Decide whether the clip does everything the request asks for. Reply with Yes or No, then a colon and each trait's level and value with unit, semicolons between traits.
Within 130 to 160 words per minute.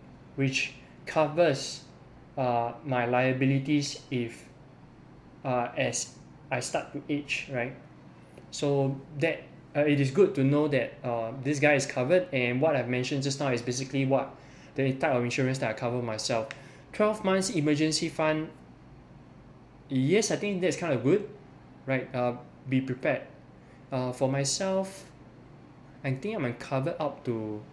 Yes: average, 150 wpm